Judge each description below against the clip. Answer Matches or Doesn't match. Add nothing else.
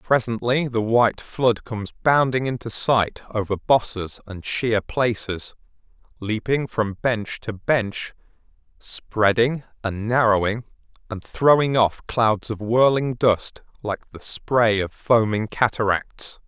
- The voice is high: Doesn't match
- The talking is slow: Matches